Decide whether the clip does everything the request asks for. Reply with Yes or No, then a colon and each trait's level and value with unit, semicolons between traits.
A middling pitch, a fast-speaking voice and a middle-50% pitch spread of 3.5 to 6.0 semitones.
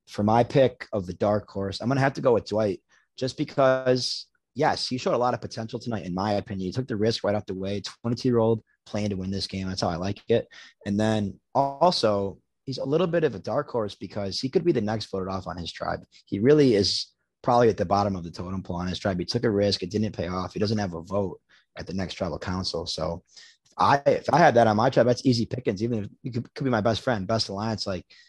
No: low, 105 Hz; fast, 270 wpm; average, 3.9 semitones